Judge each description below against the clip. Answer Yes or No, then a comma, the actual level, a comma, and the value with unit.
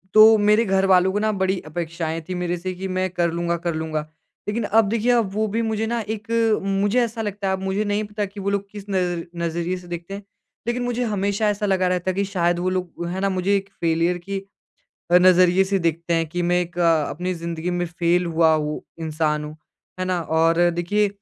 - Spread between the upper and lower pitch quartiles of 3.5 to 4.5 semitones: No, average, 2.8 semitones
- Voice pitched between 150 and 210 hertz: Yes, medium, 185 Hz